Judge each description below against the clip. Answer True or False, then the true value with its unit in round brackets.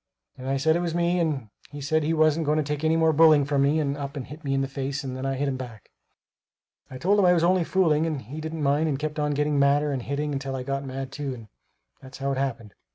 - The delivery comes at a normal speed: False (285 wpm)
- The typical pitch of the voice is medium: True (145 Hz)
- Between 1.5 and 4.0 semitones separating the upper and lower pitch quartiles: True (2.6 semitones)